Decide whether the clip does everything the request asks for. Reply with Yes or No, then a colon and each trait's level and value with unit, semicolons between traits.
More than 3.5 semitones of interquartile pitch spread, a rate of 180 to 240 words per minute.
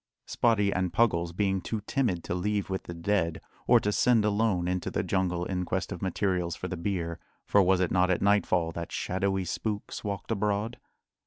No: narrow, 2.6 semitones; average, 190 wpm